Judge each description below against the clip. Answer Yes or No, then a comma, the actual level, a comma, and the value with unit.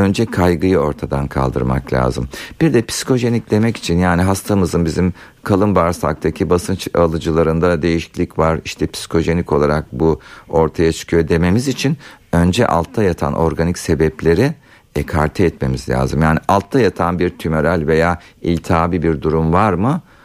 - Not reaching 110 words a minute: No, average, 135 wpm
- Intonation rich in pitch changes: No, average, 3.1 semitones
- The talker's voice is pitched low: Yes, very low, 85 Hz